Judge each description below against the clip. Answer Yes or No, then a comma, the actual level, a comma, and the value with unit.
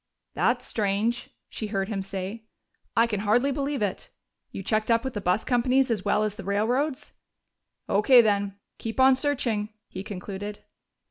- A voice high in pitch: Yes, high, 215 Hz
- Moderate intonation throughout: Yes, average, 3.4 semitones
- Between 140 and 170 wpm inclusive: Yes, average, 160 wpm